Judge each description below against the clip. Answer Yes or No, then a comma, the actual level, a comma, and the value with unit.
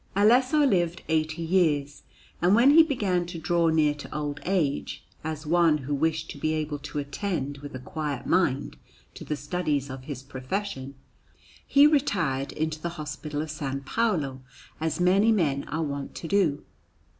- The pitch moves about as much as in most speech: Yes, average, 4.0 semitones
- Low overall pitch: No, medium, 155 Hz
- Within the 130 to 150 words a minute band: No, average, 170 wpm